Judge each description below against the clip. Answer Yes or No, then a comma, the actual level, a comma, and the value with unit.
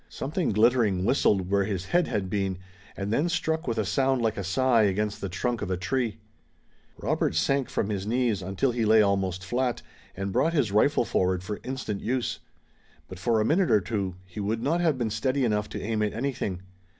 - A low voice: Yes, low, 110 Hz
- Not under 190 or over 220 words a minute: Yes, fast, 205 wpm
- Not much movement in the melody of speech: No, average, 4.8 semitones